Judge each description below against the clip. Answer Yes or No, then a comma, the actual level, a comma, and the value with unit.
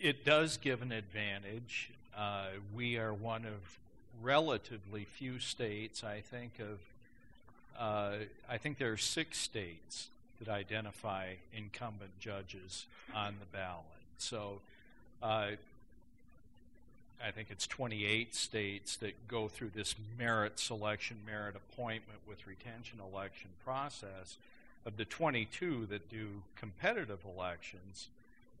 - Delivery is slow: Yes, slow, 115 wpm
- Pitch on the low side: Yes, low, 105 Hz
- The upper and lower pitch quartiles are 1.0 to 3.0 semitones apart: Yes, average, 2.7 semitones